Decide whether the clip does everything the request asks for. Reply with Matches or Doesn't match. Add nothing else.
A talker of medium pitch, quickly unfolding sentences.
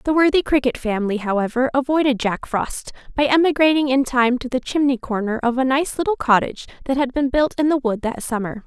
Doesn't match